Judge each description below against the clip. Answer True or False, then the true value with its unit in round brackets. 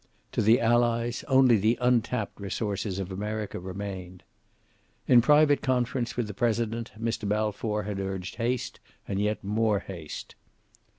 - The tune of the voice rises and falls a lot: False (3.1 semitones)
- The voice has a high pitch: False (110 Hz)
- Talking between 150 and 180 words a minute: False (135 wpm)